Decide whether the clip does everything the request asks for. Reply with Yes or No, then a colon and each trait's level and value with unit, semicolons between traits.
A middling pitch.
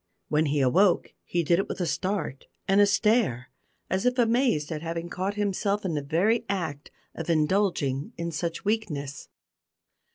Yes: medium, 175 Hz